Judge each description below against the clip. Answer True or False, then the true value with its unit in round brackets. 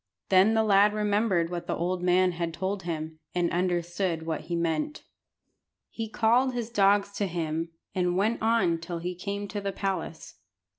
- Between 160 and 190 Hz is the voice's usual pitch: True (185 Hz)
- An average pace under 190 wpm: True (170 wpm)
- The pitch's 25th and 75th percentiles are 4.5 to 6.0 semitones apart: False (3.3 semitones)